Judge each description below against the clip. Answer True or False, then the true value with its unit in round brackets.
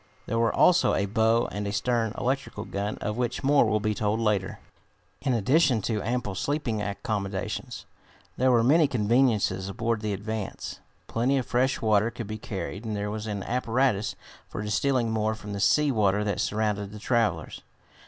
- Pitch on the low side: True (110 Hz)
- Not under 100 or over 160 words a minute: False (175 wpm)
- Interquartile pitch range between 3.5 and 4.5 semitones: False (2.9 semitones)